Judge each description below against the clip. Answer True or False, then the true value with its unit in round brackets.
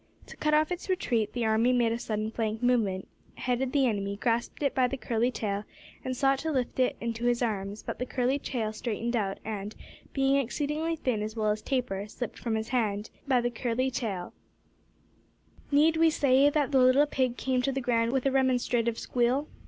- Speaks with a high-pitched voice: True (245 Hz)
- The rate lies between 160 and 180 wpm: False (190 wpm)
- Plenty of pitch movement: False (3.4 semitones)